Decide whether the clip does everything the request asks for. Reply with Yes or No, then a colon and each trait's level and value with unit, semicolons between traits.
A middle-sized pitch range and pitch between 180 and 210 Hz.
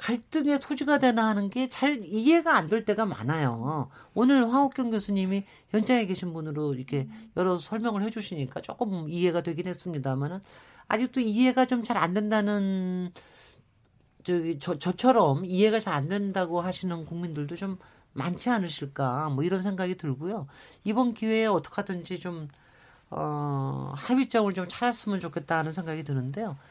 No: wide, 5.9 semitones; medium, 185 Hz